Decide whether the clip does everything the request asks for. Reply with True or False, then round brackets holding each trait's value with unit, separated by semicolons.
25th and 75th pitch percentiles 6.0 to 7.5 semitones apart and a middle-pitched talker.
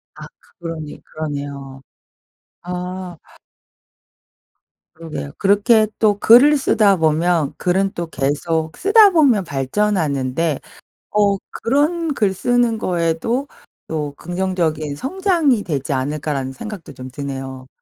True (6.7 semitones; 175 Hz)